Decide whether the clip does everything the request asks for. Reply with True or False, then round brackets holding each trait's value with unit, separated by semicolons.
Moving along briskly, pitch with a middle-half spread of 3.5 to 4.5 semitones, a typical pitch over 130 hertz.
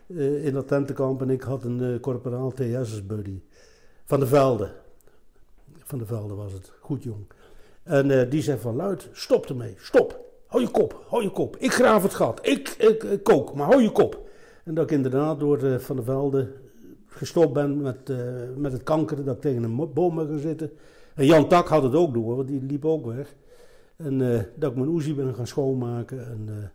True (220 wpm; 3.8 semitones; 140 Hz)